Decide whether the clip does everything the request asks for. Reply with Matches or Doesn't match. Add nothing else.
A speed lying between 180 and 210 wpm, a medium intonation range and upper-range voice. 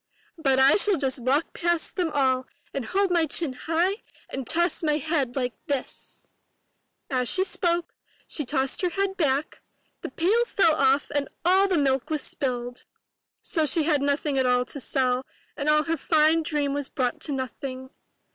Matches